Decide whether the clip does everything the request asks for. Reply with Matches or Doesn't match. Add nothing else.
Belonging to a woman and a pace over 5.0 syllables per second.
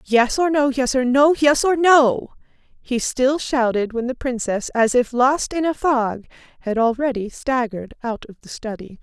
Doesn't match